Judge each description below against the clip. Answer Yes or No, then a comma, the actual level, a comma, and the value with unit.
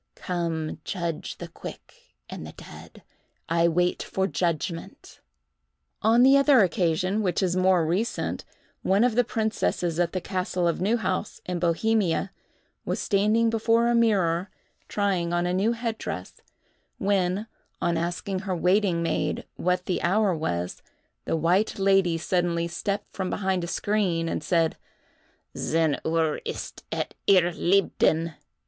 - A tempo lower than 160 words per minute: Yes, average, 140 wpm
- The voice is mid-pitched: Yes, medium, 180 Hz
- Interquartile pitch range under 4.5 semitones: Yes, average, 3.3 semitones